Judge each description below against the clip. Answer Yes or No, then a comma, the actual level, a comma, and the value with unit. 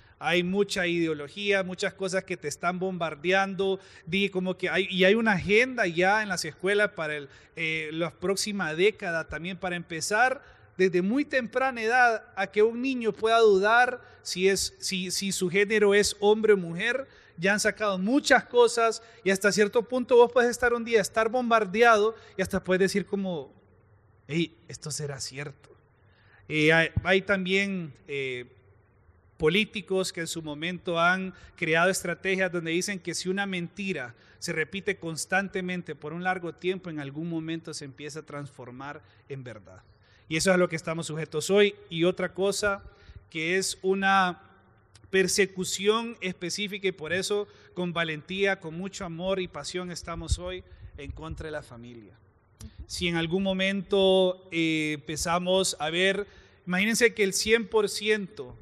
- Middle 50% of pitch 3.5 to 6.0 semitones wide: Yes, average, 4.4 semitones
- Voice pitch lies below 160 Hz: No, medium, 185 Hz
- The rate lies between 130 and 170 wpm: Yes, average, 160 wpm